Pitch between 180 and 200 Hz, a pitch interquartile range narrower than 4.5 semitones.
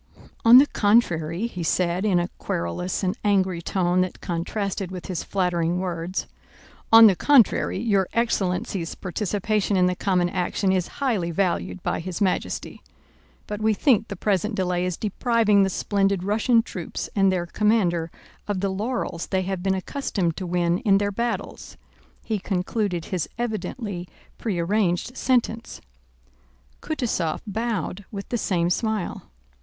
Yes: high, 190 Hz; average, 3.2 semitones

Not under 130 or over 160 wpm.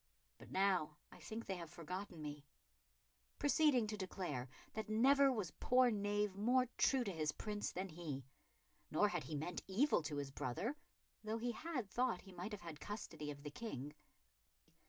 No: average, 175 wpm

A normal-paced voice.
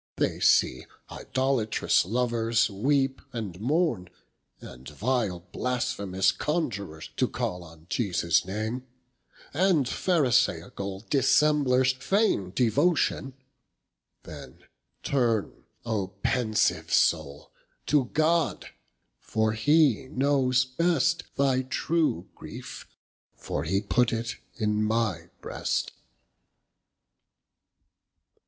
No: slow, 90 wpm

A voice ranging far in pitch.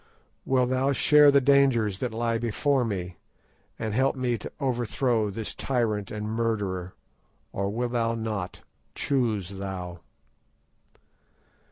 No: average, 3.9 semitones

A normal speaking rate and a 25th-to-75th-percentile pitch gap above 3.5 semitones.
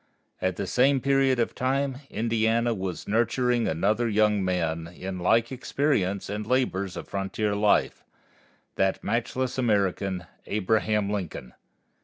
No: slow, 125 wpm; average, 4.0 semitones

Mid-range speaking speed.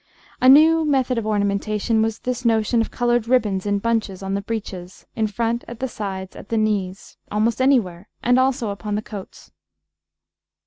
Yes: average, 175 wpm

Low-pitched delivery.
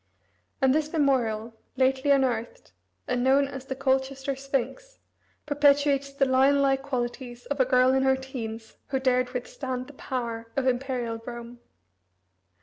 No: very high, 265 Hz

